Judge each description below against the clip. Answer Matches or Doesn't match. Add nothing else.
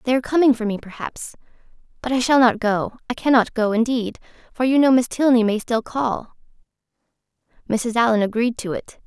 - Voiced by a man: Doesn't match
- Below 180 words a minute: Matches